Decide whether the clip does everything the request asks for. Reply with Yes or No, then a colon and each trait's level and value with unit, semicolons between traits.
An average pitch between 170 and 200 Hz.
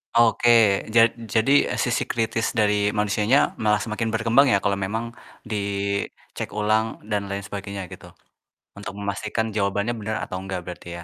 No: low, 105 Hz